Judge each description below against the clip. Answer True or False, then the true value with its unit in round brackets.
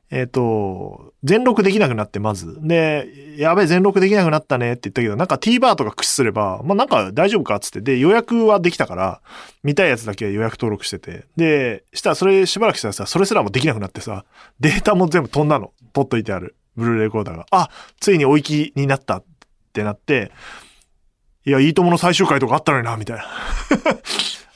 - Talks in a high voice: False (140 Hz)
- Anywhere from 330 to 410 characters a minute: False (435 characters per minute)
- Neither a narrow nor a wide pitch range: False (8.5 semitones)